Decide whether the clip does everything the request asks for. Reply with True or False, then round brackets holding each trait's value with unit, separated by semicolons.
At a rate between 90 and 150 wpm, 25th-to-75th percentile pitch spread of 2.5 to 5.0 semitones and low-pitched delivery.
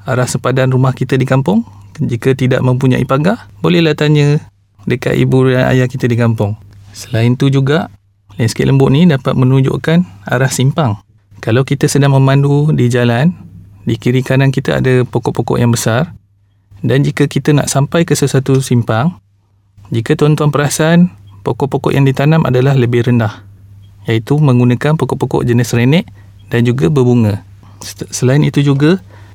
True (145 wpm; 4.1 semitones; 130 Hz)